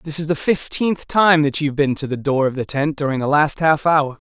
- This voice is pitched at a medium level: Yes, medium, 150 Hz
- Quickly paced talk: Yes, fast, 280 wpm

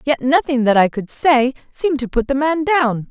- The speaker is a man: No, female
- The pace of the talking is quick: Yes, fast, 230 wpm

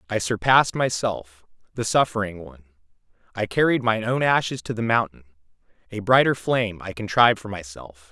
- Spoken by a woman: No, male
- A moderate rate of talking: Yes, average, 155 wpm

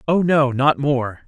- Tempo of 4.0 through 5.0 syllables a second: No, 3.7 syllables/s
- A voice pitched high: No, medium, 140 Hz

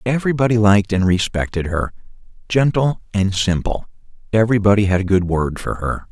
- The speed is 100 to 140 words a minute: Yes, slow, 135 wpm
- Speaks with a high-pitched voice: No, low, 105 Hz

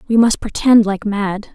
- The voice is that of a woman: Yes, female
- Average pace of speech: Yes, average, 195 wpm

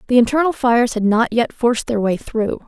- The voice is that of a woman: Yes, female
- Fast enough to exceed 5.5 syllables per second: Yes, 5.7 syllables/s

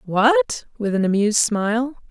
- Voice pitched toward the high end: Yes, high, 230 Hz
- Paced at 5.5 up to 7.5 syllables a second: No, 4.7 syllables/s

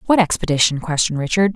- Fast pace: No, average, 155 wpm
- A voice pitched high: No, medium, 170 Hz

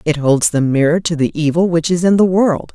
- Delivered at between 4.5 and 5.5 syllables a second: Yes, 5.3 syllables/s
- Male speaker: No, female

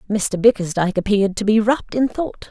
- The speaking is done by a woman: Yes, female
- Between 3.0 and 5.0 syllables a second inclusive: No, 6.0 syllables/s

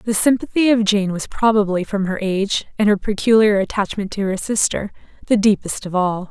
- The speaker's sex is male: No, female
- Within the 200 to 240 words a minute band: No, average, 190 wpm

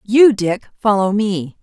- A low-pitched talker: No, high, 210 Hz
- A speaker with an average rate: Yes, average, 150 wpm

